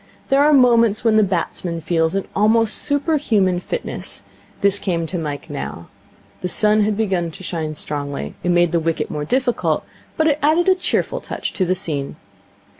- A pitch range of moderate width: No, wide, 6.0 semitones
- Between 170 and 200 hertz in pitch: Yes, high, 190 Hz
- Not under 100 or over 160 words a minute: No, average, 185 wpm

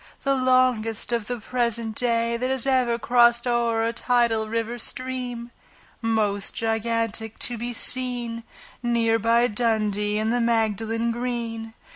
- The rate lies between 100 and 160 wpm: Yes, slow, 135 wpm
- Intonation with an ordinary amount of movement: No, narrow, 1.4 semitones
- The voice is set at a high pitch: Yes, high, 235 Hz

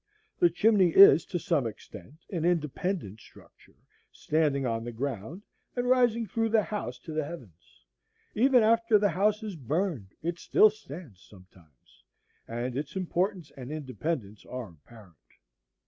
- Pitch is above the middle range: No, medium, 155 Hz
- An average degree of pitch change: No, wide, 8.9 semitones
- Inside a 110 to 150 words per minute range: Yes, average, 145 wpm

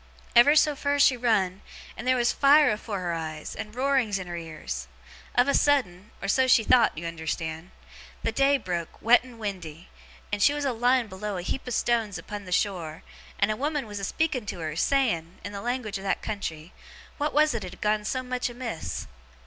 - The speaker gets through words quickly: Yes, fast, 210 wpm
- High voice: Yes, high, 215 Hz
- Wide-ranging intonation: Yes, wide, 6.0 semitones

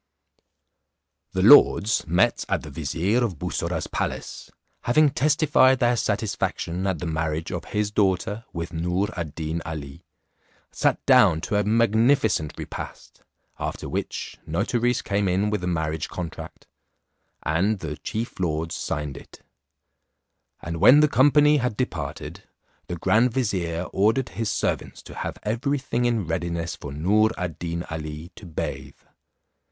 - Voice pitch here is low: Yes, very low, 95 Hz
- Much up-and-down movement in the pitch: Yes, wide, 5.9 semitones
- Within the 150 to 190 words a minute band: No, average, 140 wpm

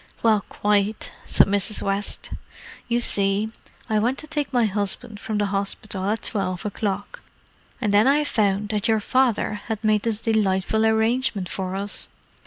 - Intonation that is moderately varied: No, narrow, 2.0 semitones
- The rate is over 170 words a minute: No, average, 160 wpm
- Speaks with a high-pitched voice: Yes, high, 210 Hz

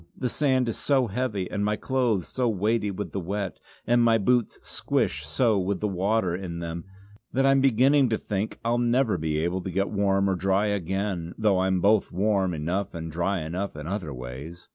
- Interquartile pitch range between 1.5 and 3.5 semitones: No, average, 4.2 semitones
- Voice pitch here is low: Yes, low, 100 Hz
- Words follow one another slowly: No, fast, 205 wpm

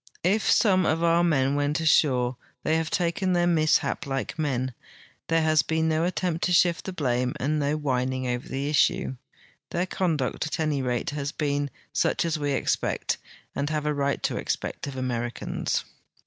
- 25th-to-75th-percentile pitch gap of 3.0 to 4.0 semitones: Yes, average, 3.6 semitones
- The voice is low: No, medium, 150 Hz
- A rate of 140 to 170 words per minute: No, average, 180 wpm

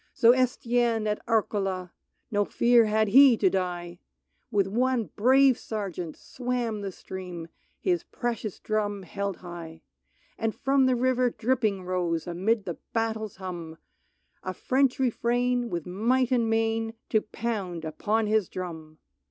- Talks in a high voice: Yes, high, 215 Hz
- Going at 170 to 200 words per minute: No, average, 145 wpm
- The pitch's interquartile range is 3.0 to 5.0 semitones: Yes, average, 4.6 semitones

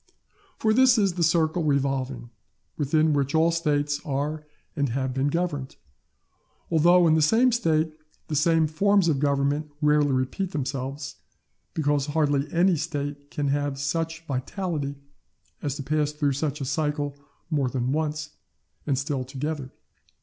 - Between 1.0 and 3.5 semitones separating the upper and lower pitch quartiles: Yes, narrow, 2.5 semitones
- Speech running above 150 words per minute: No, average, 145 wpm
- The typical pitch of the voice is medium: Yes, medium, 150 Hz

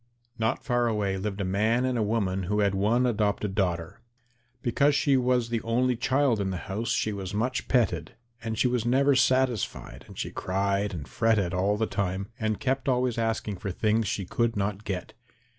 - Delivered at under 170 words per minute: No, average, 195 wpm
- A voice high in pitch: No, low, 110 Hz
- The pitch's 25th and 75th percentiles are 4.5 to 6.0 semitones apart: No, average, 3.7 semitones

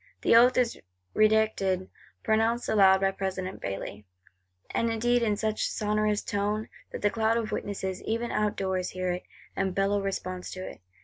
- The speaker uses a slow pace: No, average, 160 wpm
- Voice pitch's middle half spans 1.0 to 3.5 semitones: Yes, average, 2.7 semitones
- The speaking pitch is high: Yes, high, 200 Hz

